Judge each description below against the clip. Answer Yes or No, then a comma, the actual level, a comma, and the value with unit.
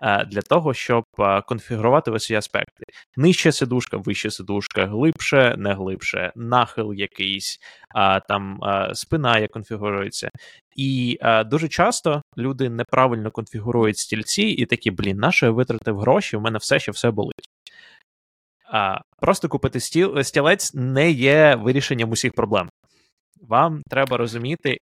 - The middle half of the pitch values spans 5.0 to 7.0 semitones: No, average, 4.3 semitones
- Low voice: Yes, low, 120 Hz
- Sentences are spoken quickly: No, average, 135 wpm